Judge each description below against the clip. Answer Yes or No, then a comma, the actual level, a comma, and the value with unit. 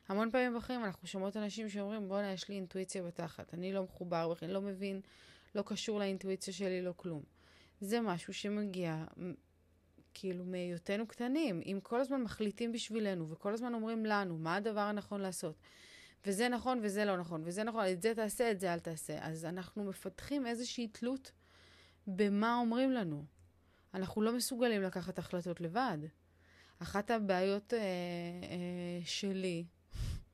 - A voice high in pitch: Yes, high, 195 Hz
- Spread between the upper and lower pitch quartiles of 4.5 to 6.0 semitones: No, average, 3.9 semitones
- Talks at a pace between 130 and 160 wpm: Yes, fast, 150 wpm